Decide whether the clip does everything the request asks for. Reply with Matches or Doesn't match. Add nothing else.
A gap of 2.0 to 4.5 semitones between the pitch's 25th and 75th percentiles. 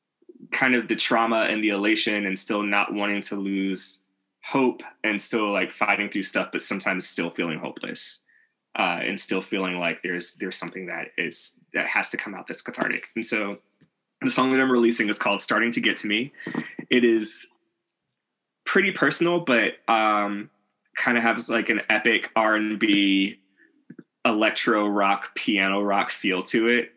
Matches